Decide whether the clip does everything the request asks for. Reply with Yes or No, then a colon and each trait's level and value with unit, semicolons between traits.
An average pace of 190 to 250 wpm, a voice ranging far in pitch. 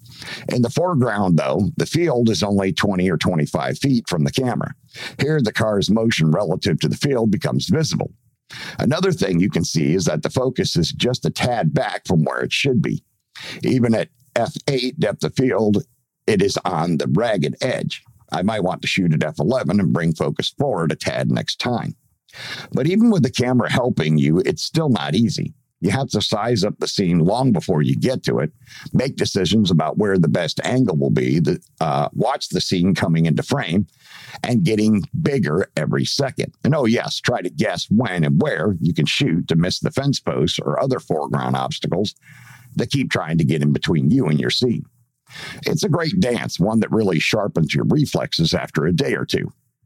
Yes: average, 195 wpm; wide, 8.3 semitones